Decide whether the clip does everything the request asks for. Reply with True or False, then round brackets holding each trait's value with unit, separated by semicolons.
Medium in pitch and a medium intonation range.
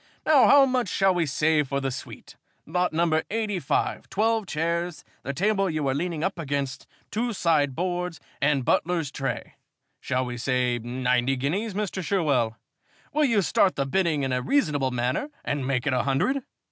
False (155 Hz; 6.1 semitones)